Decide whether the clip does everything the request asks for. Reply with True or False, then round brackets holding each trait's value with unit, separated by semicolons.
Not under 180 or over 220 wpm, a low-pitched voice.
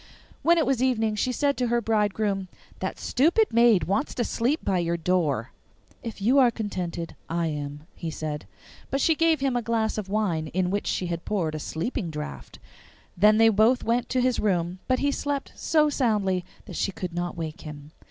False (200 wpm; 210 Hz)